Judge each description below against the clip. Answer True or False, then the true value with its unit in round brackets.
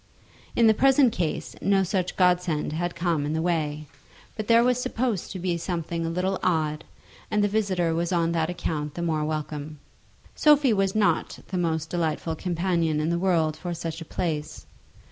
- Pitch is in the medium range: True (170 Hz)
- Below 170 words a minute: False (185 wpm)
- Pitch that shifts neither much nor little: True (3.2 semitones)